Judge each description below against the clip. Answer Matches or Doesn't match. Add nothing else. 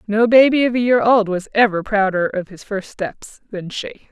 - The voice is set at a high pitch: Matches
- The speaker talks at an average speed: Doesn't match